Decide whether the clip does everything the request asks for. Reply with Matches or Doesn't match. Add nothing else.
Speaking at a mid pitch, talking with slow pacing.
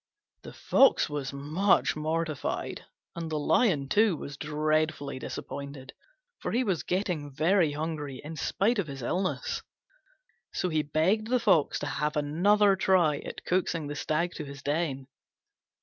Doesn't match